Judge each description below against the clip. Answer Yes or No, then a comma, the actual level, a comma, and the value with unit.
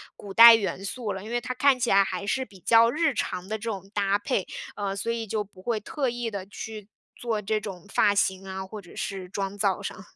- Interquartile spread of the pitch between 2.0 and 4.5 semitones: Yes, average, 2.9 semitones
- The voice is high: Yes, high, 205 Hz